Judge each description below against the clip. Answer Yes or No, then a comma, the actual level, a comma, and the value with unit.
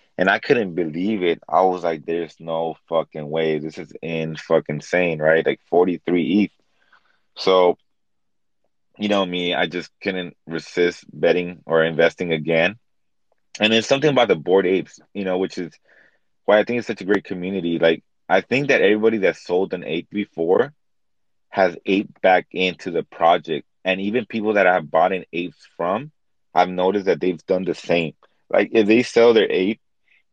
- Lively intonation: No, average, 4.0 semitones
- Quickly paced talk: No, average, 180 wpm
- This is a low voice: Yes, very low, 90 Hz